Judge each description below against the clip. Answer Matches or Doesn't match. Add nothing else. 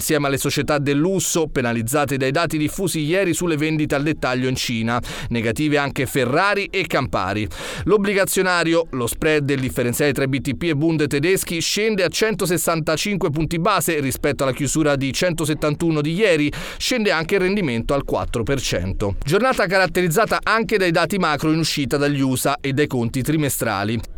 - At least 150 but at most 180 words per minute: Matches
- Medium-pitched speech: Matches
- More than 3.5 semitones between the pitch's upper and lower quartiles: Matches